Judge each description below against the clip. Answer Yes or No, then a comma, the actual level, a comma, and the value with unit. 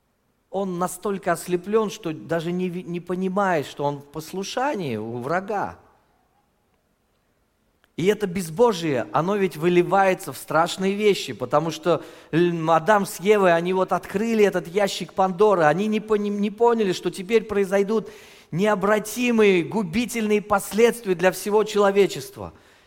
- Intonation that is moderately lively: Yes, average, 3.8 semitones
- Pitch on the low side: No, high, 190 Hz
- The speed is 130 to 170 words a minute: No, average, 120 wpm